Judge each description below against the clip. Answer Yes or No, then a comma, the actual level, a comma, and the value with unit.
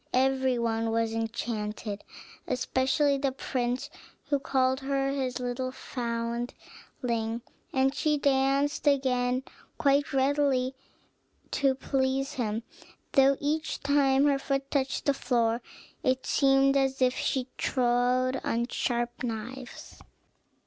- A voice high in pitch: Yes, very high, 260 Hz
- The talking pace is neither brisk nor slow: No, slow, 115 wpm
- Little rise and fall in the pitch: Yes, narrow, 2.1 semitones